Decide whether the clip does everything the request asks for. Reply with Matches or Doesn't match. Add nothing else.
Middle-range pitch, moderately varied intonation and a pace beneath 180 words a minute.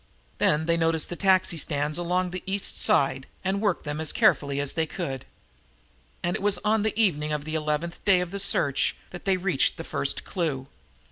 Doesn't match